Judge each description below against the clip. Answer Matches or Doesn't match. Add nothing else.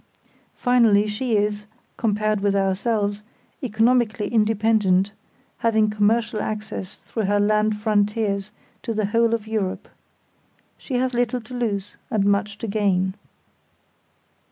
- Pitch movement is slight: Matches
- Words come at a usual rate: Doesn't match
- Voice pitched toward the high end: Matches